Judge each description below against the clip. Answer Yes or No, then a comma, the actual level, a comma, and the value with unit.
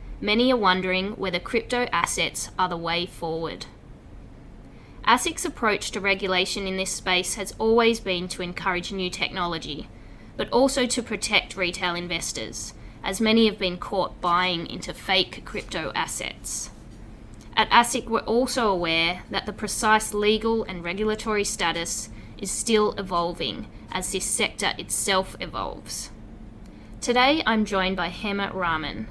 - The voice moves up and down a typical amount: Yes, average, 3.6 semitones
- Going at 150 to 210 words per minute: No, slow, 135 wpm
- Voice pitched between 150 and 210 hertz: Yes, high, 190 Hz